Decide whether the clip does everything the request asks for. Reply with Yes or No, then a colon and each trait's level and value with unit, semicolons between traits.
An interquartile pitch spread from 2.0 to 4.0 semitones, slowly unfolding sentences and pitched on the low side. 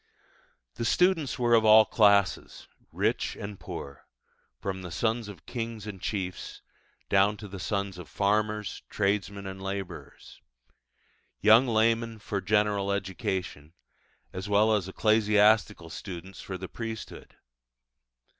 Yes: narrow, 2.4 semitones; slow, 125 wpm; low, 105 Hz